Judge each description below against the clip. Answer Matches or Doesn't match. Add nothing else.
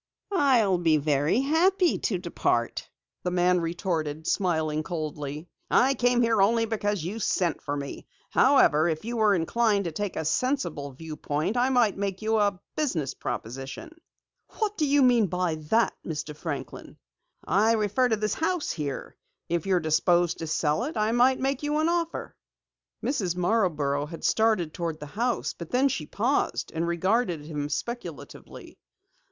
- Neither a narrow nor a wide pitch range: Doesn't match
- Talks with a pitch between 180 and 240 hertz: Matches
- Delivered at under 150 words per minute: Doesn't match